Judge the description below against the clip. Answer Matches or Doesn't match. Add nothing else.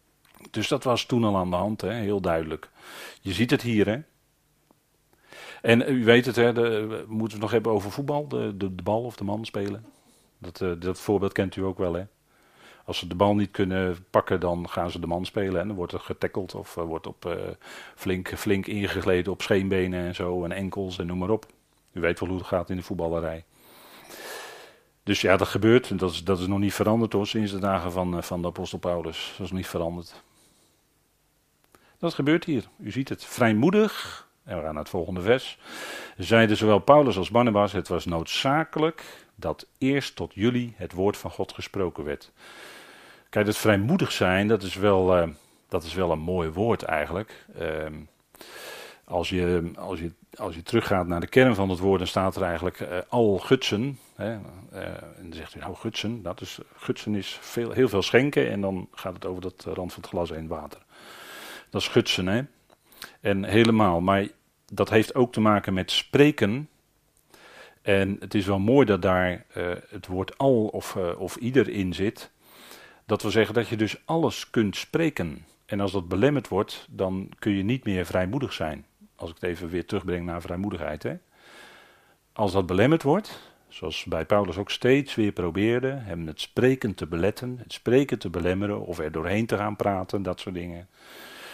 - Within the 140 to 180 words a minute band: Doesn't match